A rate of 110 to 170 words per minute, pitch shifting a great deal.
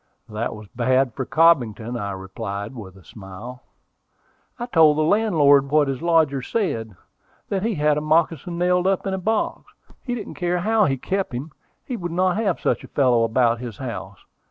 No: average, 185 wpm; wide, 7.4 semitones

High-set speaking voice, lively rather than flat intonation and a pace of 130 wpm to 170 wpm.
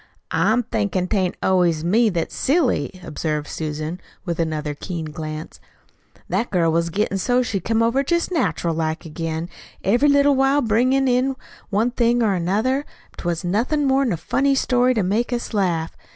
Yes: high, 205 Hz; wide, 6.9 semitones; average, 165 wpm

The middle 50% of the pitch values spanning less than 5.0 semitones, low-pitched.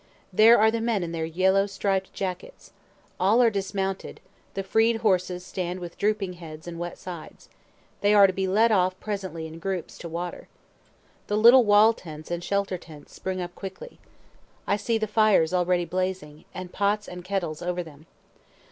No: average, 2.9 semitones; high, 190 Hz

